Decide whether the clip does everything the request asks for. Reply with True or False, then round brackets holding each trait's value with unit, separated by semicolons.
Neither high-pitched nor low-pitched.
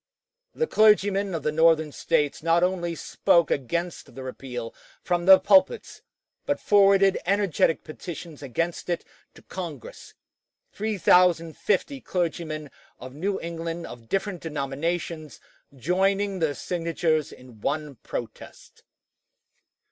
True (170 Hz)